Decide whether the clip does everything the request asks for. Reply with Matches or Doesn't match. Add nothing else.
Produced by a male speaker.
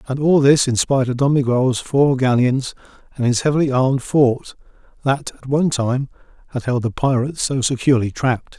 Matches